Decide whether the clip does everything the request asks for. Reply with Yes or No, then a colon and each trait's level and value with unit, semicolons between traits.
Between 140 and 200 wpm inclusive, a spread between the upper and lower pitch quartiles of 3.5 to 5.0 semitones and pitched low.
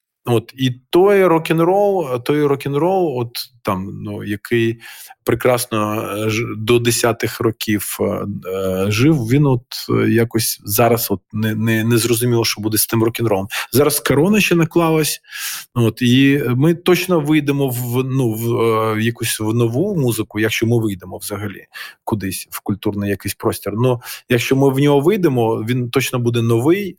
Yes: fast, 155 wpm; average, 4.3 semitones; low, 120 Hz